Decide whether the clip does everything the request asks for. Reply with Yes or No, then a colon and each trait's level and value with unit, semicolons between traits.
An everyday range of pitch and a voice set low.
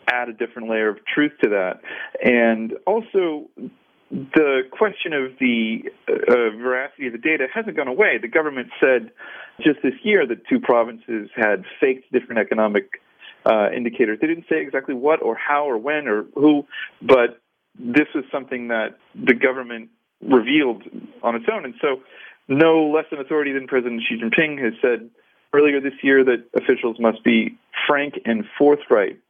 Yes: average, 4.5 semitones; low, 130 Hz